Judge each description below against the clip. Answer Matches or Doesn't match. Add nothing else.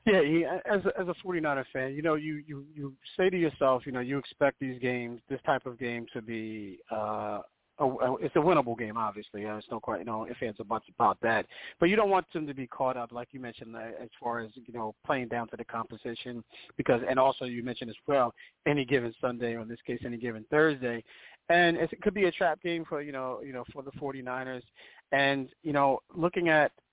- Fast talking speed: Matches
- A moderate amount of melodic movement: Matches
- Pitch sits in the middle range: Doesn't match